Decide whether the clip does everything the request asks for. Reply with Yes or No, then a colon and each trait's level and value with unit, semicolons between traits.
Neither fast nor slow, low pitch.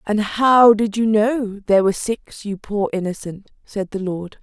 No: average, 190 wpm; high, 210 Hz